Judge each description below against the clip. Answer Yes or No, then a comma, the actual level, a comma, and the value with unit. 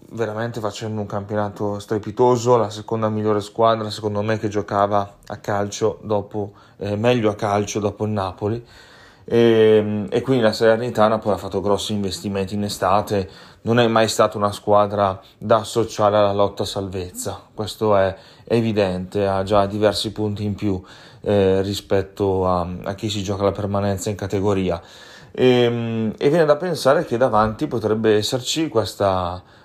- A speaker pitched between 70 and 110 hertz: Yes, low, 105 Hz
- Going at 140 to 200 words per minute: Yes, average, 155 wpm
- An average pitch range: No, narrow, 1.8 semitones